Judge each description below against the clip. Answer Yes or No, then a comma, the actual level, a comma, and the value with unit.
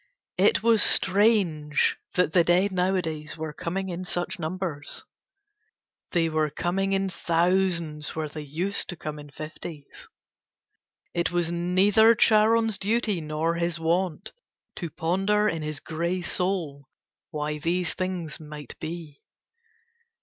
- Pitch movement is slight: No, average, 3.5 semitones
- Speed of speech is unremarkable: No, slow, 130 wpm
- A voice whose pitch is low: No, medium, 175 Hz